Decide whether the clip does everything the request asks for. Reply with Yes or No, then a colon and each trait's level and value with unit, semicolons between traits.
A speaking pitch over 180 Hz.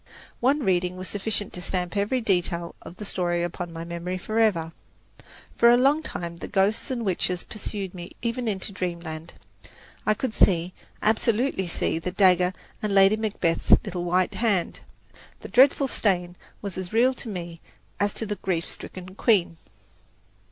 Yes: high, 190 Hz